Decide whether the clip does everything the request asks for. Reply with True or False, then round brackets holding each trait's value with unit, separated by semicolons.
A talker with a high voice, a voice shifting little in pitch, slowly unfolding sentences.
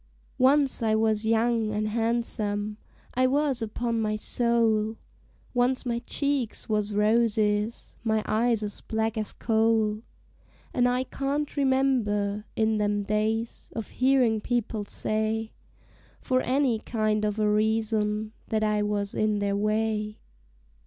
True (220 Hz; 2.0 semitones; 130 wpm)